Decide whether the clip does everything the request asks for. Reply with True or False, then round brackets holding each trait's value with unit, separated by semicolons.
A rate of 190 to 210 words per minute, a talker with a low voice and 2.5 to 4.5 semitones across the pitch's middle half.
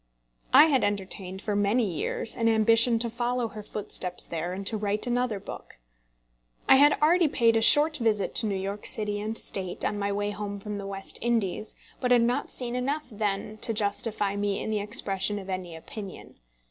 False (195 wpm; 210 Hz; 2.8 semitones)